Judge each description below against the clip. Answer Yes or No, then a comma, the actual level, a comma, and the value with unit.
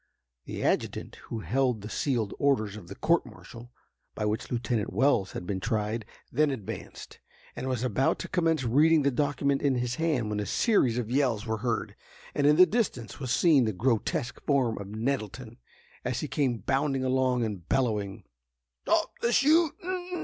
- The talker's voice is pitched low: Yes, low, 125 Hz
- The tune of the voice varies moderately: Yes, average, 4.6 semitones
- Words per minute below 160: No, average, 175 wpm